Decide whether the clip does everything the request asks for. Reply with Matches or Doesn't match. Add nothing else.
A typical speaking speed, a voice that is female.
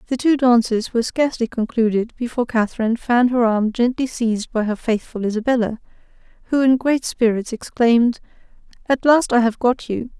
Matches